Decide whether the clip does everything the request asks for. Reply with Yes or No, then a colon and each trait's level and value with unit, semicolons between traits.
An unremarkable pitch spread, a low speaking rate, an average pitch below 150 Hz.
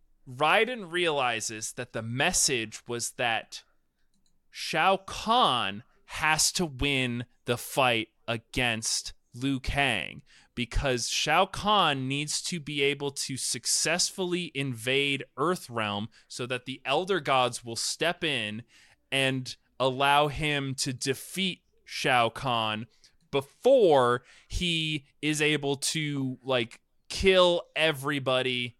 Yes: average, 4.0 semitones; slow, 105 wpm; low, 135 Hz